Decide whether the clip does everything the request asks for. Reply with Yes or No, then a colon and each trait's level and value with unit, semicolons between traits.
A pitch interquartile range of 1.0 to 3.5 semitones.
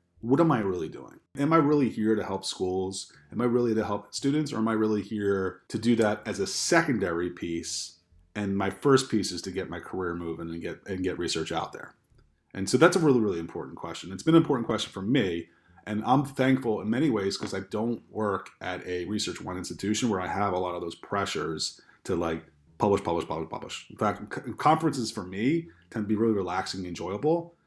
No: average, 4.6 semitones